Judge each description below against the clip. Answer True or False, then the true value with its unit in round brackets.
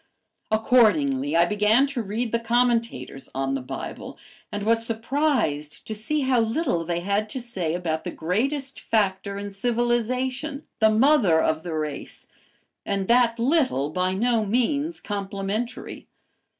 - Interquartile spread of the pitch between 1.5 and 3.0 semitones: False (5.3 semitones)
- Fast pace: False (140 wpm)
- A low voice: False (220 Hz)